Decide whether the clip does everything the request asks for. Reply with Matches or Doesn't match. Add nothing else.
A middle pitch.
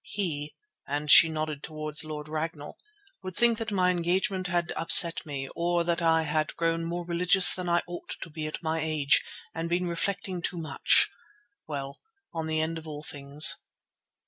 Matches